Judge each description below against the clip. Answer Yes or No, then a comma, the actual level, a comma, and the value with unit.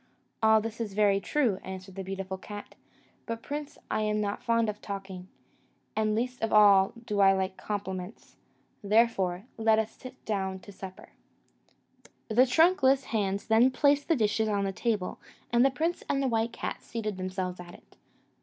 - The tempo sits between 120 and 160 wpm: No, average, 170 wpm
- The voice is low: No, high, 210 Hz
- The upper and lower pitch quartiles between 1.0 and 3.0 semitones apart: No, average, 3.4 semitones